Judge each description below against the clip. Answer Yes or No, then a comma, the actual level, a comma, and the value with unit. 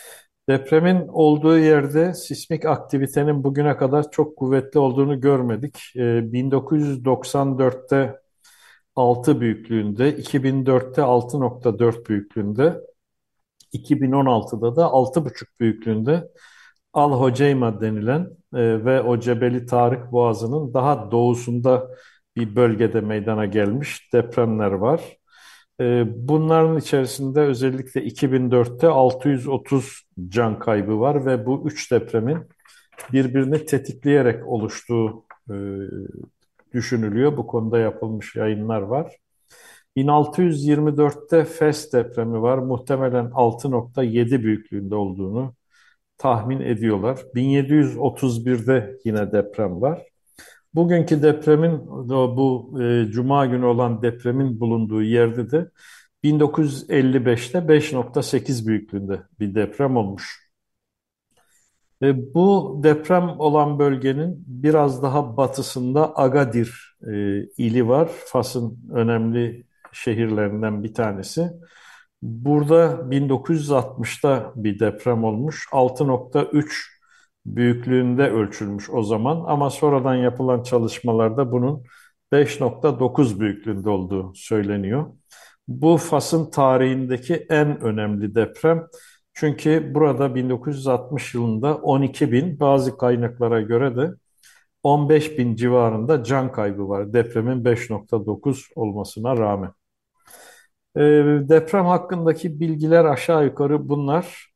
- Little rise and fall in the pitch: No, average, 4.1 semitones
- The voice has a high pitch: No, low, 130 Hz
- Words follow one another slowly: Yes, slow, 90 wpm